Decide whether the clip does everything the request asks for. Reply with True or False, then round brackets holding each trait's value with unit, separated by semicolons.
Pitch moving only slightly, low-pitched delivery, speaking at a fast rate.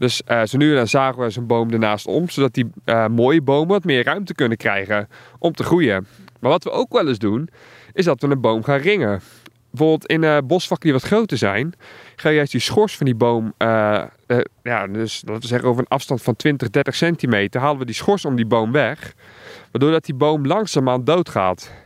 False (4.7 semitones; 130 Hz; 230 wpm)